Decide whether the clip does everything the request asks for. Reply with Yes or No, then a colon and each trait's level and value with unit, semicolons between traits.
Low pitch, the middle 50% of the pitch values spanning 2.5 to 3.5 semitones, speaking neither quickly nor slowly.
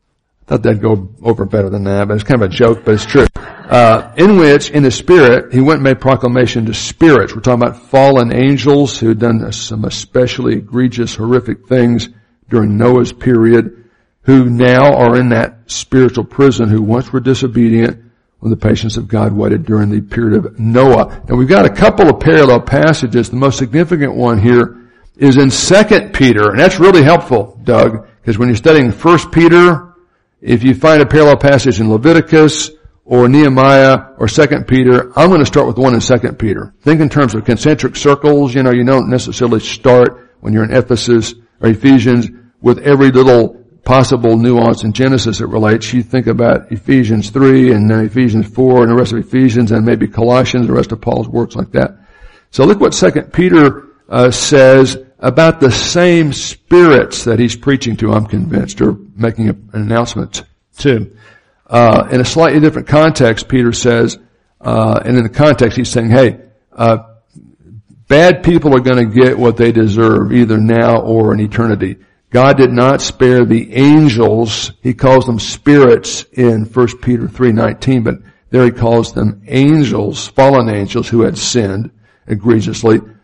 Yes: low, 120 Hz; average, 2.9 semitones; average, 180 wpm